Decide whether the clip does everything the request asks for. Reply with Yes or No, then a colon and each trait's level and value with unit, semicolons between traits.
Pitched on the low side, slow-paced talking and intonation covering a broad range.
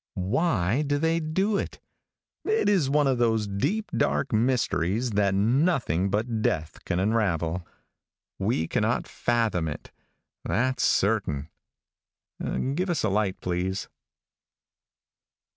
Yes: low, 110 Hz; slow, 115 wpm; wide, 6.9 semitones